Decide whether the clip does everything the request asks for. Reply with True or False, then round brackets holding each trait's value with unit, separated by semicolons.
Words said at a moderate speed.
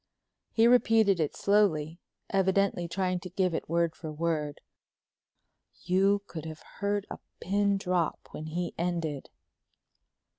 False (125 wpm)